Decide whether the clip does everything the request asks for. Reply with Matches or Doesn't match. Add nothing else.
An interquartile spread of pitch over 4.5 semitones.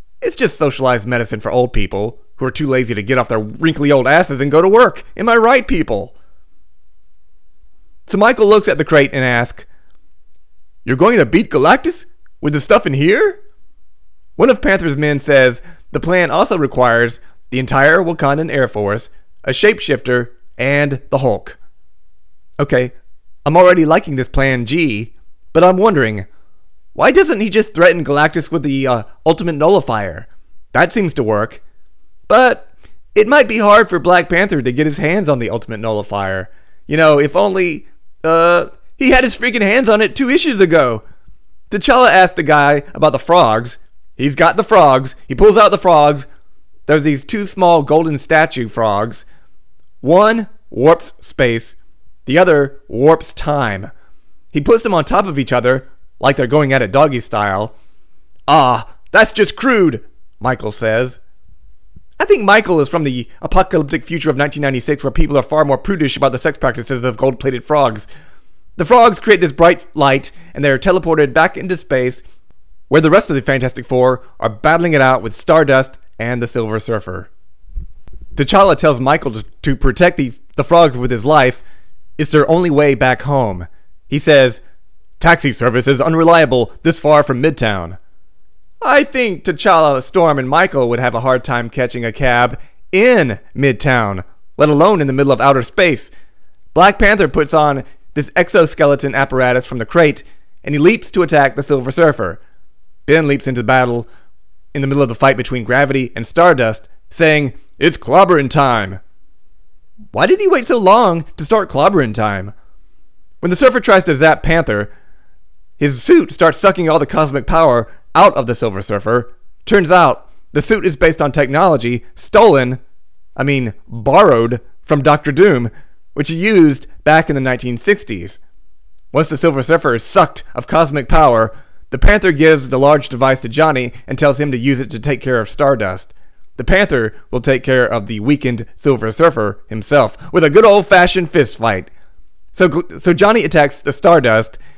Matches